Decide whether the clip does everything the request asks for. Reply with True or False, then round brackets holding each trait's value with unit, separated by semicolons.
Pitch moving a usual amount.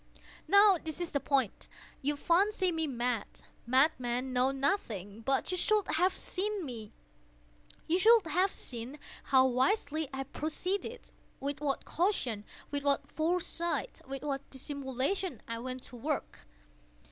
False (5.7 semitones)